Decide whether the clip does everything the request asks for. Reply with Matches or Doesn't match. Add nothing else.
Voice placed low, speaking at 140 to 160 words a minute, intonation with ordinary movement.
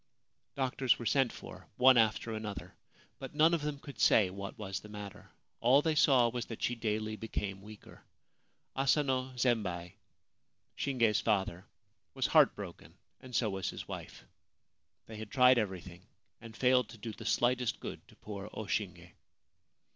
Matches